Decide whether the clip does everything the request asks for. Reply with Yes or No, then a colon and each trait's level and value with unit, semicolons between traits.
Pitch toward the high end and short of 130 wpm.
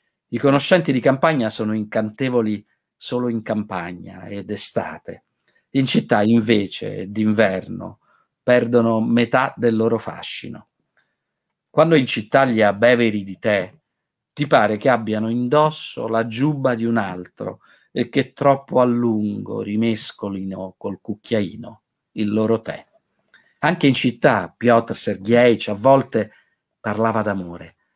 No: low, 115 Hz; average, 120 wpm